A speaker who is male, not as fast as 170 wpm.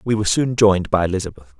No: male; fast, 225 wpm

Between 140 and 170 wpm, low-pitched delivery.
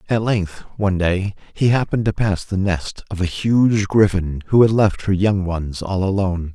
No: average, 200 wpm; low, 100 Hz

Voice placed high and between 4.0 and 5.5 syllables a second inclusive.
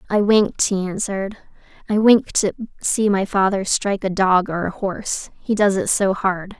Yes: high, 195 Hz; 4.8 syllables/s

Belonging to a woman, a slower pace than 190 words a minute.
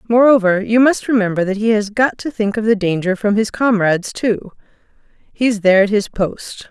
No: female; average, 195 wpm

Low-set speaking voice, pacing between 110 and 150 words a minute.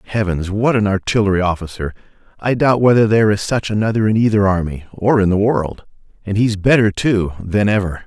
No: low, 105 Hz; average, 195 wpm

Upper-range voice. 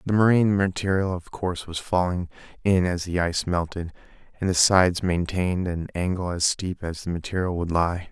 No: very low, 90 Hz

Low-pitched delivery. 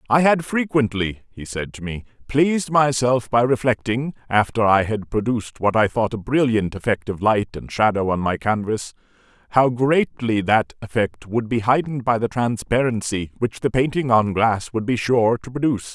Yes: low, 115 Hz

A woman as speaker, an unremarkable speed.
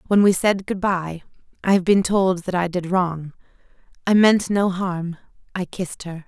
Yes: female; average, 170 wpm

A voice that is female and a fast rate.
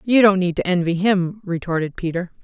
No: female; average, 195 wpm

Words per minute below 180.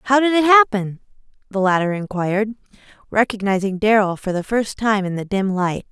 Yes: average, 170 wpm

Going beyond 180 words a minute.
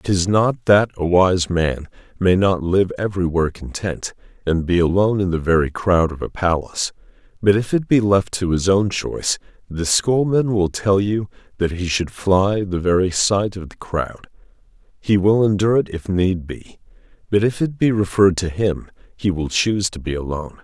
Yes: average, 190 wpm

